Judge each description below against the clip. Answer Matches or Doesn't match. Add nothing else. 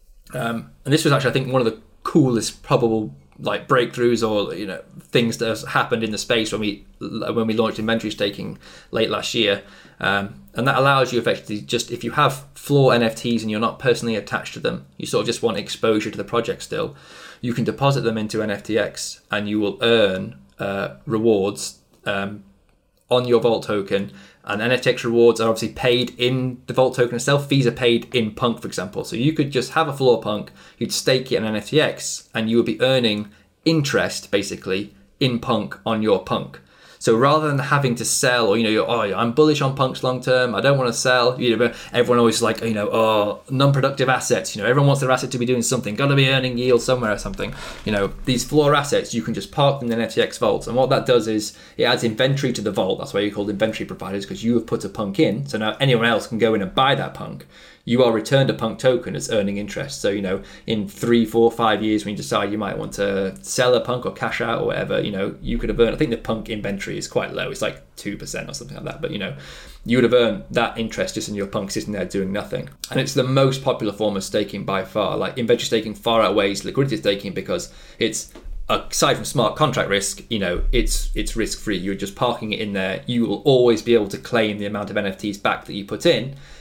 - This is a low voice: Matches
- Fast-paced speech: Matches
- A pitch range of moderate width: Matches